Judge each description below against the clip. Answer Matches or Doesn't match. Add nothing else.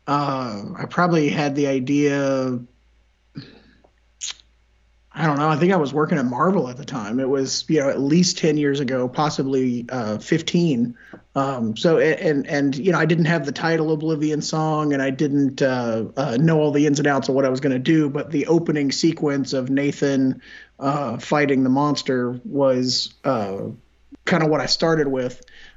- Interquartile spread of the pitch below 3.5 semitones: Matches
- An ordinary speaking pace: Matches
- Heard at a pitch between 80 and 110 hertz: Doesn't match